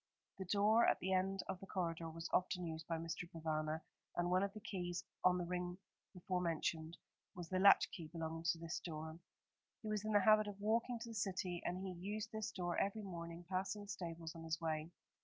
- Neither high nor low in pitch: Yes, medium, 180 Hz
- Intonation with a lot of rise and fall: No, average, 3.1 semitones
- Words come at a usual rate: No, fast, 215 wpm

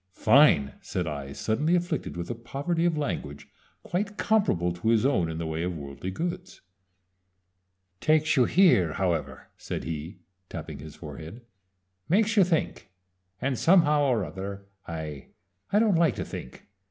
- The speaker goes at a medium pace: Yes, average, 155 wpm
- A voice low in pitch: Yes, low, 115 Hz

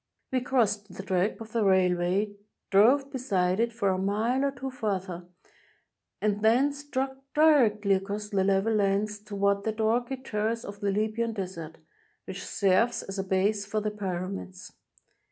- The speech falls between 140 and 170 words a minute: Yes, average, 155 wpm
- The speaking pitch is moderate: No, high, 210 Hz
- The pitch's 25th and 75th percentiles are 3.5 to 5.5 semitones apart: No, average, 3.1 semitones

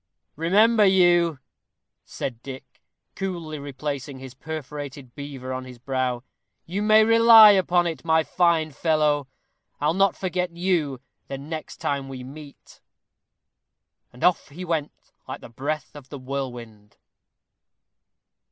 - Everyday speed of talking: No, slow, 125 wpm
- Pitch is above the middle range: No, medium, 150 Hz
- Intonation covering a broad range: No, average, 4.7 semitones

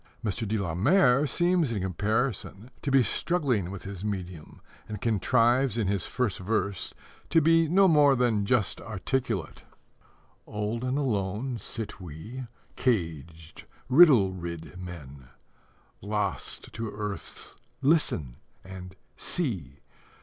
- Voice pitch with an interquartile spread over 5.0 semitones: Yes, wide, 5.6 semitones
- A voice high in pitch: No, low, 105 Hz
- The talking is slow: Yes, slow, 120 wpm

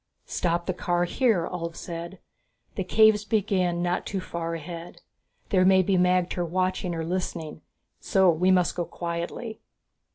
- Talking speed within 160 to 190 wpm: No, average, 150 wpm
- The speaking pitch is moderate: Yes, medium, 180 Hz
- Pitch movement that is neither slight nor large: No, narrow, 1.7 semitones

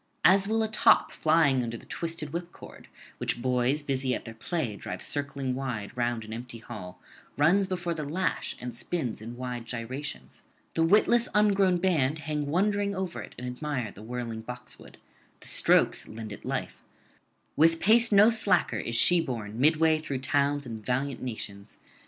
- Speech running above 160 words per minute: Yes, average, 170 wpm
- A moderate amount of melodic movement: No, wide, 6.2 semitones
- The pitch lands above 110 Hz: Yes, medium, 140 Hz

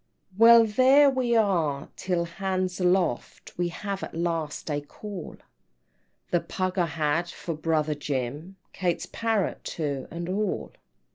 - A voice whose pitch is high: No, medium, 175 Hz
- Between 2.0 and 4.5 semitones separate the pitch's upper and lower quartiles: Yes, average, 4.0 semitones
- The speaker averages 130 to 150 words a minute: Yes, average, 140 wpm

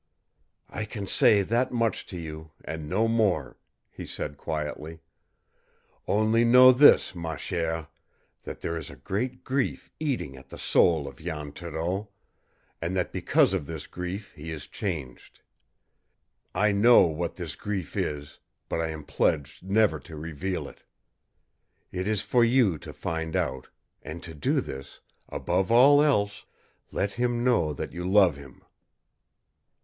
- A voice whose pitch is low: Yes, very low, 90 Hz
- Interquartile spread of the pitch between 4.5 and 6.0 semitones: Yes, wide, 5.6 semitones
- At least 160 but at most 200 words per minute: No, average, 150 wpm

